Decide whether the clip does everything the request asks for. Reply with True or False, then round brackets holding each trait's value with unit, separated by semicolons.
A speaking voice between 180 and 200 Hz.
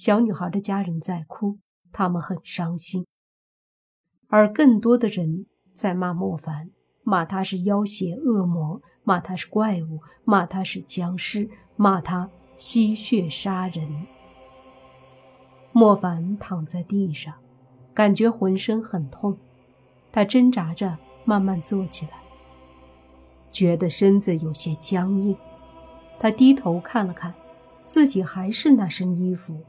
True (185 Hz)